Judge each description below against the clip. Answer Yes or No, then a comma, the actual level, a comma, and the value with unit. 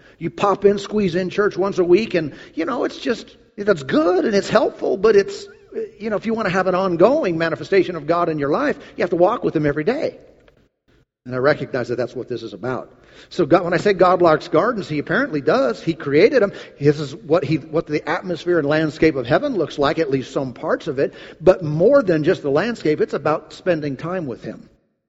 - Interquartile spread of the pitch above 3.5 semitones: Yes, average, 4.6 semitones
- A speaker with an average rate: No, fast, 235 wpm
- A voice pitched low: No, medium, 175 Hz